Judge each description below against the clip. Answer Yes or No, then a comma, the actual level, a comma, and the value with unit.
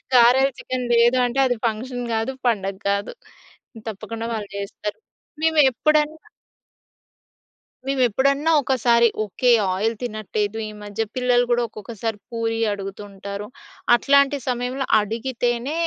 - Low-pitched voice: No, high, 235 Hz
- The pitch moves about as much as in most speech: Yes, average, 3.2 semitones